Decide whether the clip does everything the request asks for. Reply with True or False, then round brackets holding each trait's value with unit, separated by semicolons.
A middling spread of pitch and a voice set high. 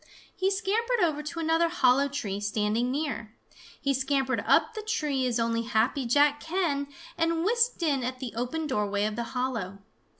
False (5.8 semitones; 275 Hz)